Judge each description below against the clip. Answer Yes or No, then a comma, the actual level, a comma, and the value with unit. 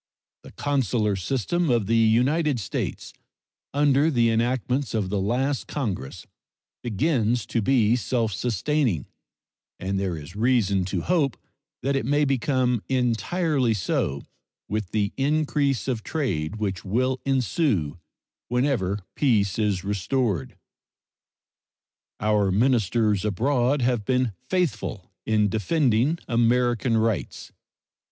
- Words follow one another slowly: Yes, slow, 115 wpm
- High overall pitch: No, low, 120 Hz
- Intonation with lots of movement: No, average, 4.6 semitones